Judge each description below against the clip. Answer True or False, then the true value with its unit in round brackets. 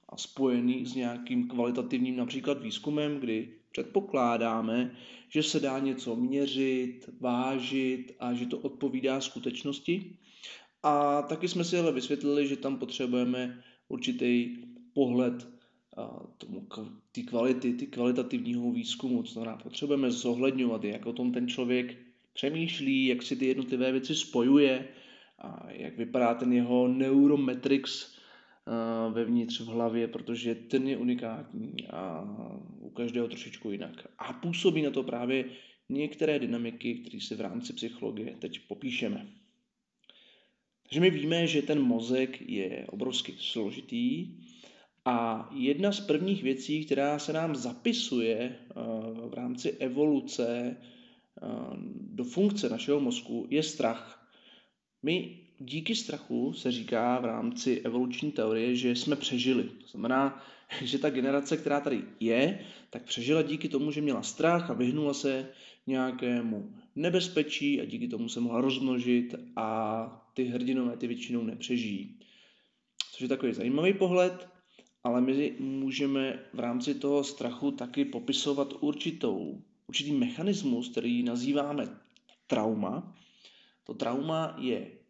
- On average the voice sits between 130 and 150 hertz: True (135 Hz)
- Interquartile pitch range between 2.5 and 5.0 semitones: False (5.7 semitones)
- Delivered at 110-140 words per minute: True (125 wpm)